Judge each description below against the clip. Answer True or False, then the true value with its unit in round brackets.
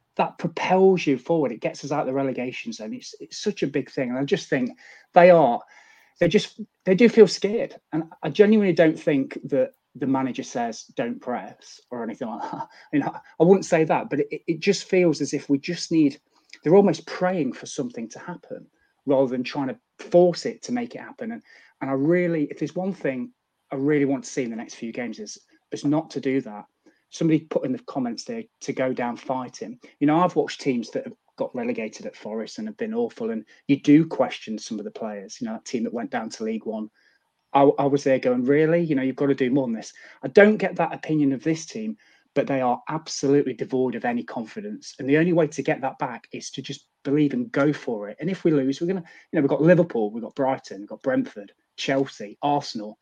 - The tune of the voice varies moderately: False (7.9 semitones)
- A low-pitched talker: False (160 Hz)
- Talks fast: True (240 wpm)